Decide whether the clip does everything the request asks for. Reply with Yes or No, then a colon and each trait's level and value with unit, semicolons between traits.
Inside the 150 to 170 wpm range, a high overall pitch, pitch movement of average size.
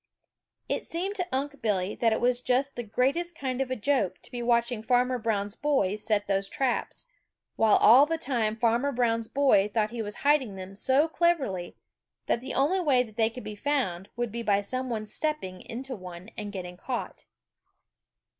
No: average, 185 wpm; high, 240 Hz; average, 4.4 semitones